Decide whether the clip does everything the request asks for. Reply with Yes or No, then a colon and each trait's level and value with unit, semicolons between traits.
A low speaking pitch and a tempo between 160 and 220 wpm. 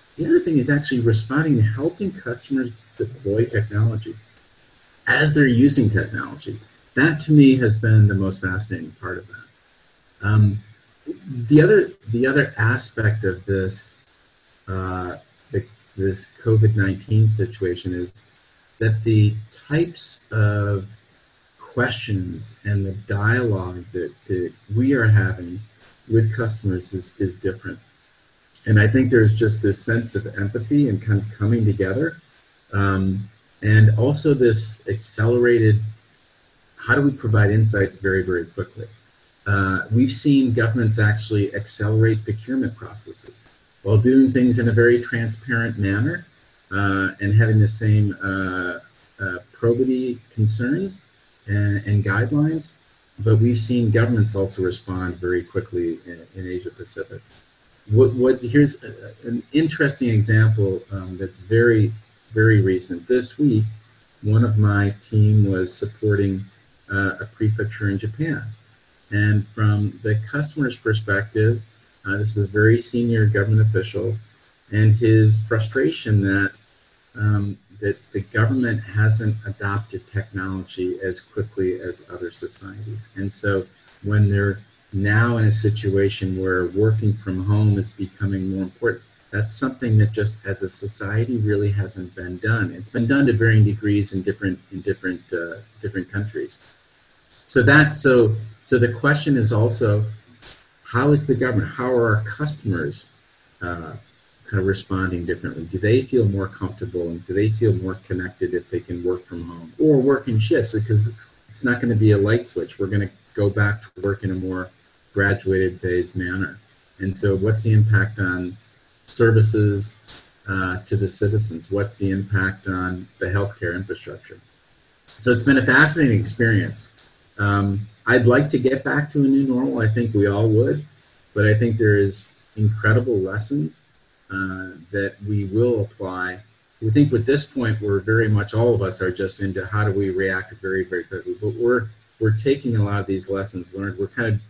No: low, 110 Hz; average, 150 wpm